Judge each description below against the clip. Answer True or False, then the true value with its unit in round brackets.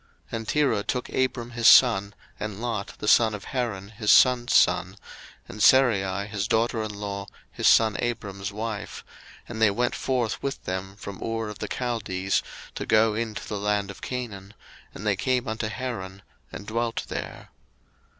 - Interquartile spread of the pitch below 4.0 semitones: True (2.9 semitones)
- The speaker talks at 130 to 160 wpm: False (170 wpm)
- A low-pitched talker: True (110 Hz)